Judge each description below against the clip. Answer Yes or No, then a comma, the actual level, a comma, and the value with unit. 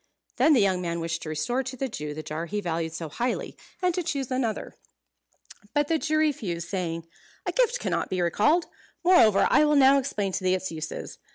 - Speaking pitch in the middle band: No, high, 205 Hz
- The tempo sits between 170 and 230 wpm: Yes, fast, 205 wpm